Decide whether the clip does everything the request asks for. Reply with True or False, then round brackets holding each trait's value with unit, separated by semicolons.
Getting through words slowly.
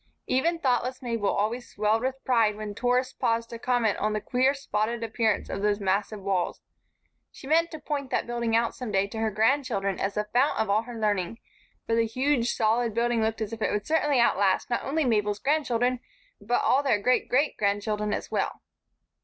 False (200 wpm)